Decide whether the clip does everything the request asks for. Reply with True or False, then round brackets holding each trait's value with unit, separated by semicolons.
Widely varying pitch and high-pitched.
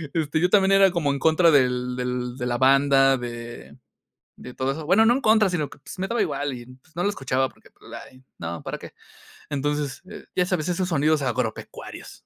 False (5.7 semitones; 140 Hz)